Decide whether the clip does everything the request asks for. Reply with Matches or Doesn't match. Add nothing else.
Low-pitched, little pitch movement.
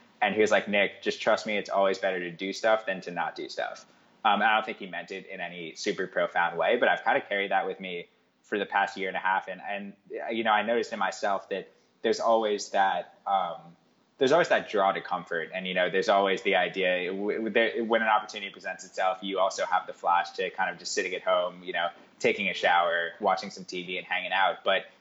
Matches